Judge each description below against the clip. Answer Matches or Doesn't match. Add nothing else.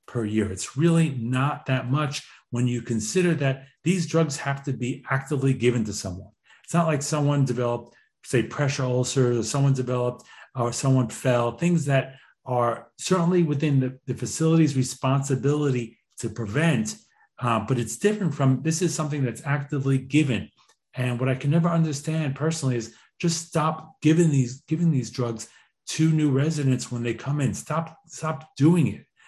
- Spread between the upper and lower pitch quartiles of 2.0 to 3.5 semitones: Doesn't match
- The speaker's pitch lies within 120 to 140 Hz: Matches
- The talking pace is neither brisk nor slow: Matches